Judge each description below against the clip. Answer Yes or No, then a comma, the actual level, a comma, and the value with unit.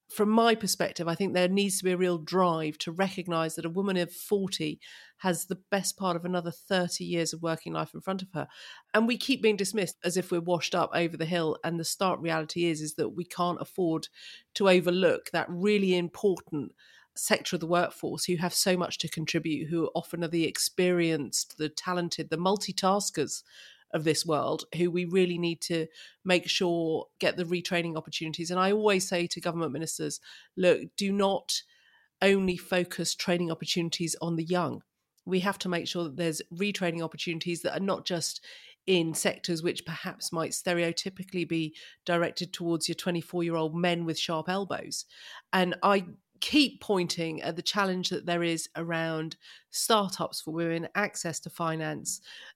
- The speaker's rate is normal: Yes, average, 180 wpm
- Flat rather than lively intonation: Yes, narrow, 2.3 semitones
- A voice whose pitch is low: No, medium, 175 Hz